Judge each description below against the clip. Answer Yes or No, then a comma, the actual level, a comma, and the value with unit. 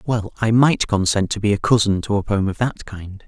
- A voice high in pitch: No, low, 105 Hz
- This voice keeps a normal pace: No, fast, 255 wpm